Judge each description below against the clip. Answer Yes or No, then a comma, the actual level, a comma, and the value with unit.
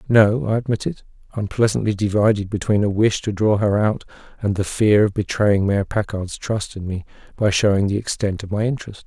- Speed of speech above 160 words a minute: Yes, average, 190 wpm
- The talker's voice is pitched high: No, low, 105 Hz